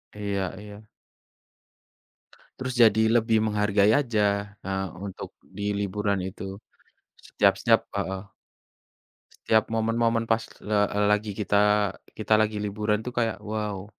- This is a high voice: No, low, 105 Hz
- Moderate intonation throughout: No, narrow, 1.5 semitones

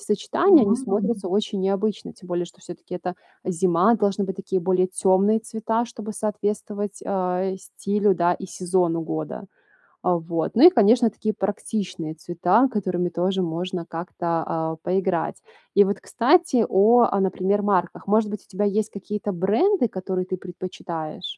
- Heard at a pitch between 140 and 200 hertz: Yes, high, 190 Hz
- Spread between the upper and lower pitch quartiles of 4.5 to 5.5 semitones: No, average, 2.8 semitones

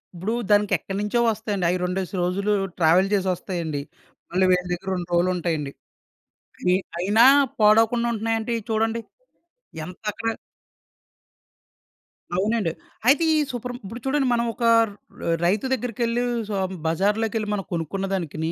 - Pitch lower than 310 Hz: Yes, high, 200 Hz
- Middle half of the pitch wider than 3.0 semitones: Yes, average, 3.9 semitones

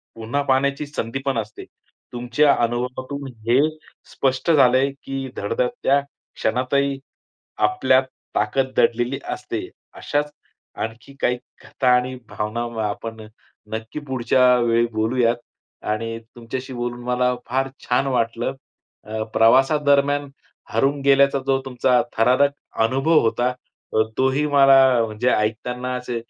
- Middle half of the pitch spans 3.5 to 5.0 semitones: No, average, 2.7 semitones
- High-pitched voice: No, low, 125 Hz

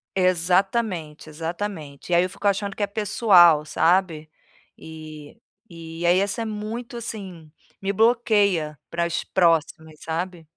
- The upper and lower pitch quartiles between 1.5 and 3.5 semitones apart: No, average, 4.0 semitones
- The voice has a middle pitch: Yes, medium, 180 Hz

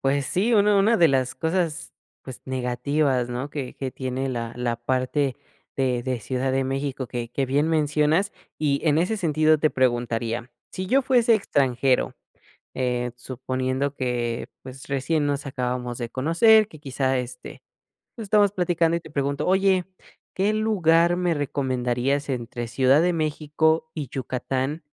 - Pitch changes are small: No, average, 4.2 semitones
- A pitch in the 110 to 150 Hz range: Yes, medium, 140 Hz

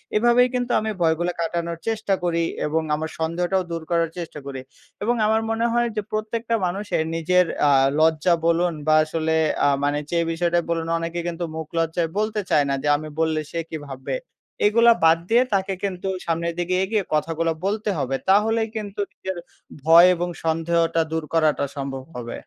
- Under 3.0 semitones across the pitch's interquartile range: No, average, 4.1 semitones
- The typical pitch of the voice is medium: Yes, medium, 170 Hz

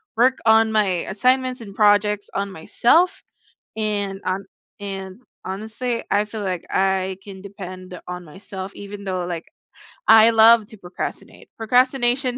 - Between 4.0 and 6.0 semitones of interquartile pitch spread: No, average, 2.8 semitones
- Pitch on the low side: No, high, 205 Hz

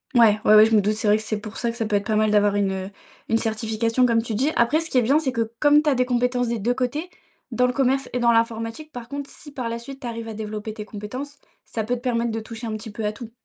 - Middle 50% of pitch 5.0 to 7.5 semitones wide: No, narrow, 2.6 semitones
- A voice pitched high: Yes, high, 230 Hz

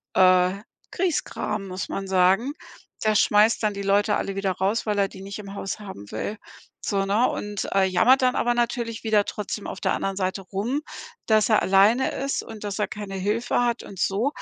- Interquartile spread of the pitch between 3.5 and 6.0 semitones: No, narrow, 2.5 semitones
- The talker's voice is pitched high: Yes, high, 205 Hz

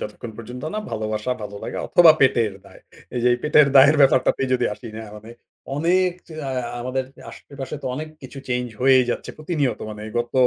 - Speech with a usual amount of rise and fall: Yes, average, 3.4 semitones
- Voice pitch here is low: Yes, low, 130 Hz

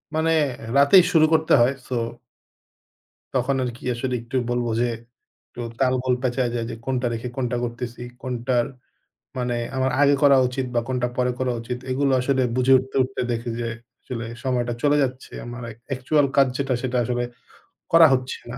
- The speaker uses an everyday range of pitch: No, narrow, 1.6 semitones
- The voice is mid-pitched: No, low, 130 Hz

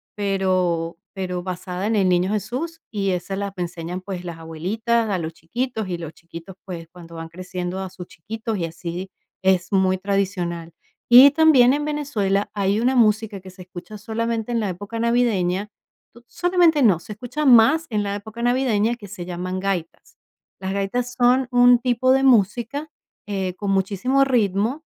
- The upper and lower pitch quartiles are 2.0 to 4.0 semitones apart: No, average, 4.7 semitones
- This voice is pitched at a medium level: No, high, 200 Hz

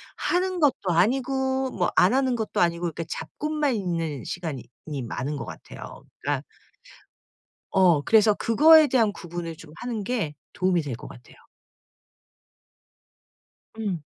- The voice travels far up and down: Yes, wide, 8.0 semitones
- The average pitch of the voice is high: Yes, high, 195 Hz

